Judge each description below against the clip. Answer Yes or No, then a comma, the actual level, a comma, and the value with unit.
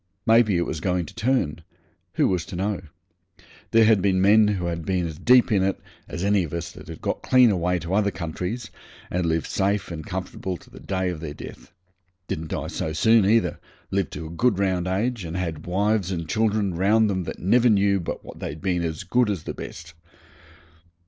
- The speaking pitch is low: Yes, very low, 95 Hz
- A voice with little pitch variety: No, average, 3.6 semitones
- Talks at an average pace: No, fast, 210 wpm